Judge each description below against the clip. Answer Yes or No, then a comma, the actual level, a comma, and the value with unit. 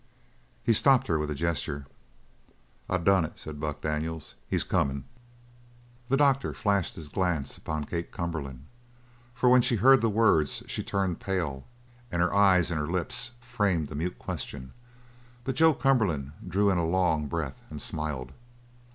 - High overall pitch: No, very low, 85 Hz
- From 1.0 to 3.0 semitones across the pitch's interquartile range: No, average, 5.2 semitones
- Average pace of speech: Yes, average, 160 wpm